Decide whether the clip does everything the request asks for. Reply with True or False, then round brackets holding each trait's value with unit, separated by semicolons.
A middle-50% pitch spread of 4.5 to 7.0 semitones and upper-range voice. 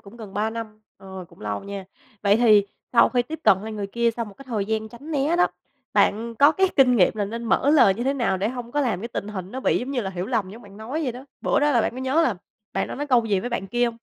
False (4.1 semitones; 230 Hz)